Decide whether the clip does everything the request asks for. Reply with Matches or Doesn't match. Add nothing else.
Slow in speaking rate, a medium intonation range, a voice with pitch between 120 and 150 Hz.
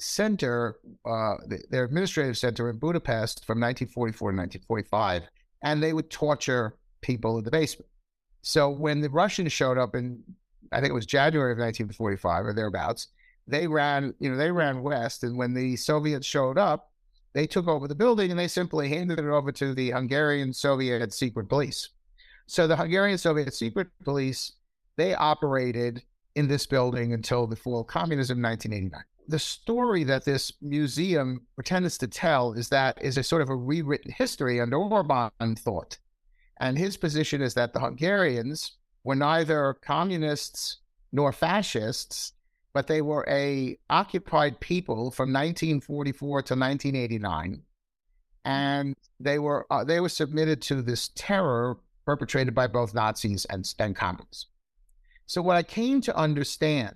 Doesn't match